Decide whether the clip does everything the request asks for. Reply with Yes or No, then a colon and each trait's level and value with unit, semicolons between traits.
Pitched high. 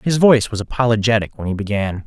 No: low, 110 Hz